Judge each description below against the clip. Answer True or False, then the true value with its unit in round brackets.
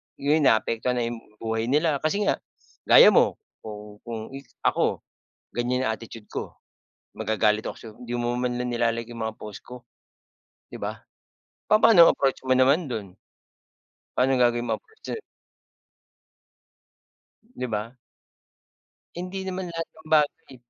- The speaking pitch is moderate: False (125 Hz)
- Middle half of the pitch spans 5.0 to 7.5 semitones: True (5.3 semitones)